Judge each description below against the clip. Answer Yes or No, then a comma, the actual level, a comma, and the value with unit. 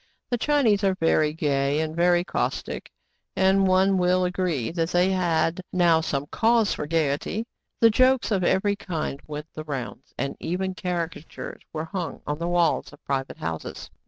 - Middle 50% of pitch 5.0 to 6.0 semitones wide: No, average, 3.7 semitones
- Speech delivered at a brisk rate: No, average, 165 wpm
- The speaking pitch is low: No, medium, 175 Hz